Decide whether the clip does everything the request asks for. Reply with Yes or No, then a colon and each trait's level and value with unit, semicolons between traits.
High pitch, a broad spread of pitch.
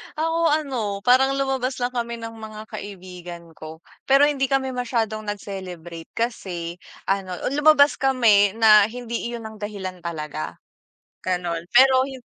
Yes: high, 220 Hz; wide, 6.0 semitones